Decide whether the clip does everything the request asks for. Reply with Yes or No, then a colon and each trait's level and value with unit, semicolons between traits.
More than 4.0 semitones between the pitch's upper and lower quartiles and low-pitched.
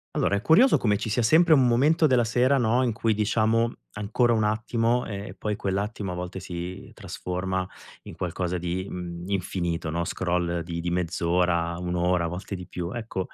Yes: average, 4.5 semitones; very low, 95 Hz